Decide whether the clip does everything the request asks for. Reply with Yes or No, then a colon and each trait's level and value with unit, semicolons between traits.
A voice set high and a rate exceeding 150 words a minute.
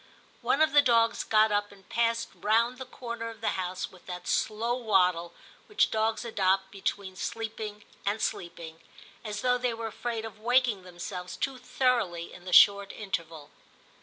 Yes: high, 215 Hz; average, 165 wpm